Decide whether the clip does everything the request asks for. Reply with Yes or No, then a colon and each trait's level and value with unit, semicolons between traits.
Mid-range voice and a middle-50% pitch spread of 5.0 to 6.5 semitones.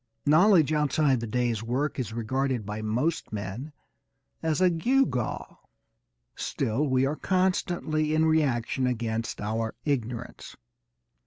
No: low, 130 Hz; average, 5.3 semitones